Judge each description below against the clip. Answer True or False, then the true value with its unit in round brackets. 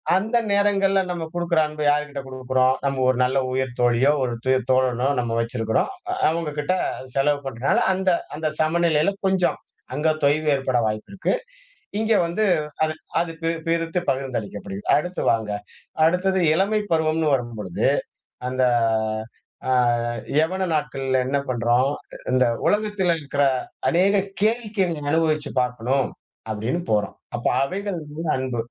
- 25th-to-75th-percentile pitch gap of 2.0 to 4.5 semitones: False (5.3 semitones)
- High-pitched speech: False (150 Hz)